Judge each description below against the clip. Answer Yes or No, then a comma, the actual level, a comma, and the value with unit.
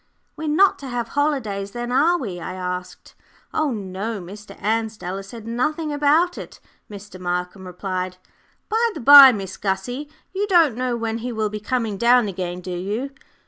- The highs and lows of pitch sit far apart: Yes, wide, 6.2 semitones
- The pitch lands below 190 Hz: No, high, 225 Hz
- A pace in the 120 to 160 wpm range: No, average, 175 wpm